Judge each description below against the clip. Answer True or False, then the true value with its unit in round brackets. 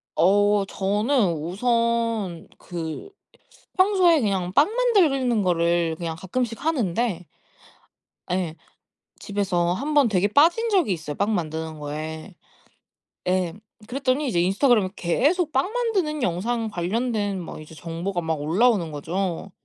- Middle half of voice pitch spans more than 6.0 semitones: True (6.9 semitones)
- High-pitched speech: True (200 Hz)